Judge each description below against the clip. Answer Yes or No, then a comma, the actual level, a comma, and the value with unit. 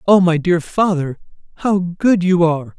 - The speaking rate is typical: Yes, average, 170 wpm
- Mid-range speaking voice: Yes, medium, 175 Hz